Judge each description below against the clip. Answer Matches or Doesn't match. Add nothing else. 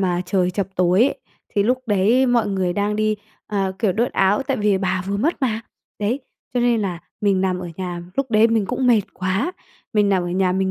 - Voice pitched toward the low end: Doesn't match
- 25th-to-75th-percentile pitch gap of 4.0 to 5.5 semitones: Doesn't match